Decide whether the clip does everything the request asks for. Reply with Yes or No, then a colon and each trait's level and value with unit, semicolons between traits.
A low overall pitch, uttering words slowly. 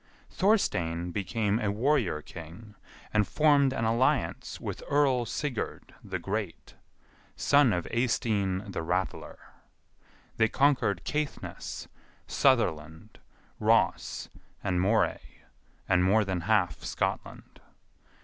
Yes: low, 105 Hz; slow, 100 wpm